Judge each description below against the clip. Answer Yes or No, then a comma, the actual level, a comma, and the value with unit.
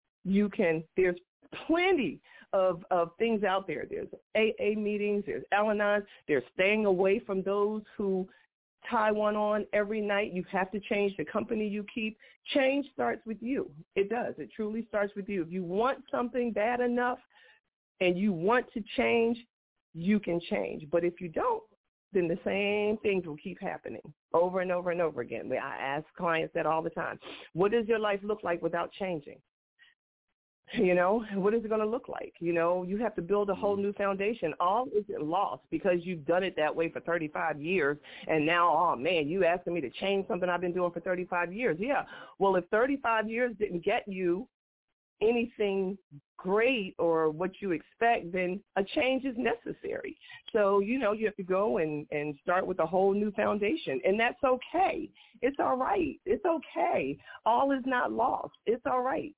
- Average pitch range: Yes, average, 4.5 semitones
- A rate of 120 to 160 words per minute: No, average, 190 wpm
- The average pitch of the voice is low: No, high, 205 Hz